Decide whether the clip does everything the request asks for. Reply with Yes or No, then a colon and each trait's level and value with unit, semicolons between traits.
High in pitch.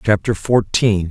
No: low, 100 Hz